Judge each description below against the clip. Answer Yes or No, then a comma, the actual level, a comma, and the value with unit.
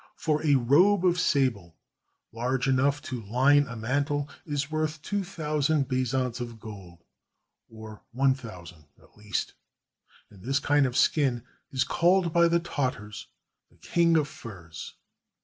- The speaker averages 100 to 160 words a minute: Yes, average, 150 wpm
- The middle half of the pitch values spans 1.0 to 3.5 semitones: No, average, 4.9 semitones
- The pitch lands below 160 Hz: Yes, low, 135 Hz